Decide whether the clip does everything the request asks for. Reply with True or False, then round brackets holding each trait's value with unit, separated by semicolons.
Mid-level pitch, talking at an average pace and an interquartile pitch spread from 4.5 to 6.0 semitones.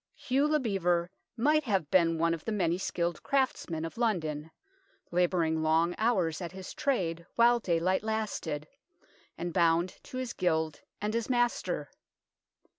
True (180 Hz; 145 wpm; 5.5 semitones)